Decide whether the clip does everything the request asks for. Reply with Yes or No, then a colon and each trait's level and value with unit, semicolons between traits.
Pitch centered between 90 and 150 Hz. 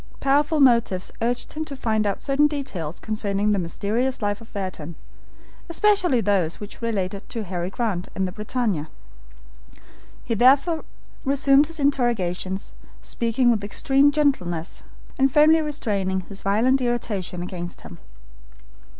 No: high, 225 Hz